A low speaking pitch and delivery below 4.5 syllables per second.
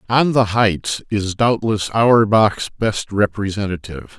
Yes: low, 105 Hz; 4.2 syllables/s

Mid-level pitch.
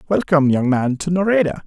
Yes: medium, 160 Hz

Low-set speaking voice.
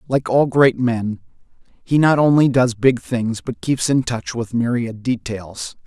Yes: low, 120 Hz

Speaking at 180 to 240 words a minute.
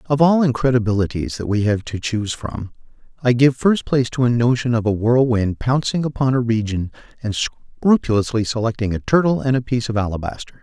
Yes: average, 185 wpm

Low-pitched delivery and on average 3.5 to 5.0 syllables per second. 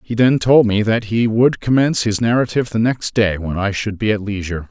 No: low, 110 Hz; 5.7 syllables/s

